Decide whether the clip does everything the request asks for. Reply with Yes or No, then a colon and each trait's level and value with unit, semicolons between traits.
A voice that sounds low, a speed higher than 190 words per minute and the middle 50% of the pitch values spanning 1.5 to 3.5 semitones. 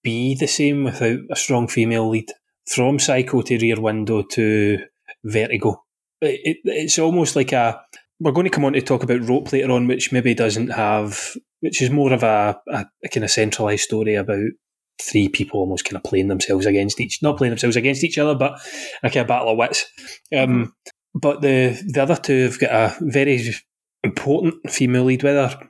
No: low, 130 Hz; average, 200 wpm; average, 4.2 semitones